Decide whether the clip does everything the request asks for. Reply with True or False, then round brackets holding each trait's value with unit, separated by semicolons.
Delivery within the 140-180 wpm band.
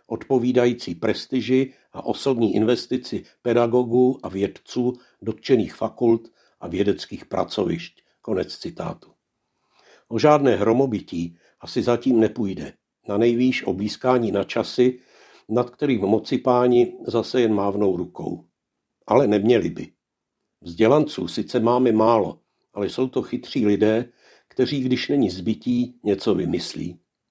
False (115 wpm)